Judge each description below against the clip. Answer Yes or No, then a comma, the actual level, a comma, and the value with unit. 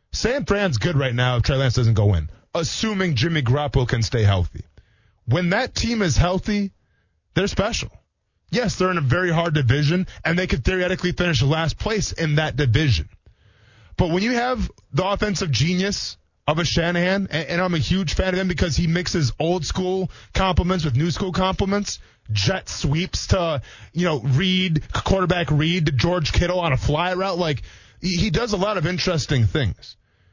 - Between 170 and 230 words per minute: Yes, average, 180 wpm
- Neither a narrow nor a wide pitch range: No, wide, 6.9 semitones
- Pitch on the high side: No, medium, 160 Hz